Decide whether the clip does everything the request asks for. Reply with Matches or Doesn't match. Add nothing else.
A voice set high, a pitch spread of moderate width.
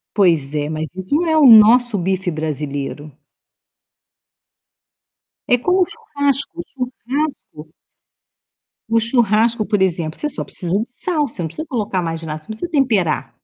Doesn't match